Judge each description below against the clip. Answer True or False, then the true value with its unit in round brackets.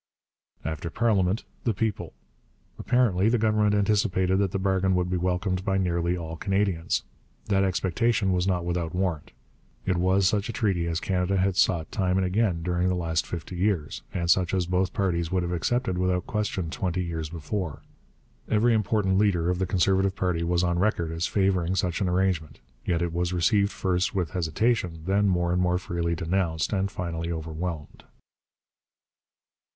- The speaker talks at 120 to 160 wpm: False (170 wpm)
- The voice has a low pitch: True (90 Hz)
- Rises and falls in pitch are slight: True (2.1 semitones)